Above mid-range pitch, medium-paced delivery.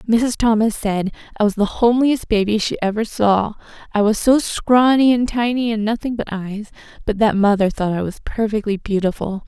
Yes: high, 215 Hz; average, 185 wpm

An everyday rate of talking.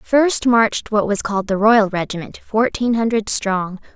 Yes: average, 165 wpm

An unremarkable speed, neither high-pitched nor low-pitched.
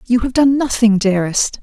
No: average, 185 wpm; high, 230 Hz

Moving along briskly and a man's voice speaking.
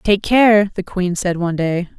No: fast, 210 wpm; female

